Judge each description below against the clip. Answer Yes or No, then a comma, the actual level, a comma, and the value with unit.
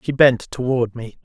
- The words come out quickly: No, average, 195 wpm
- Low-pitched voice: Yes, low, 125 Hz